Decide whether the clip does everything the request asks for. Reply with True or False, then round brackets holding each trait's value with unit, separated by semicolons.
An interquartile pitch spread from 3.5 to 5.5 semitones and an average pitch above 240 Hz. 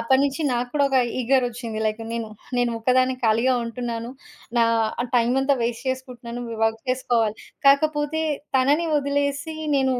False (3.0 semitones; 255 Hz)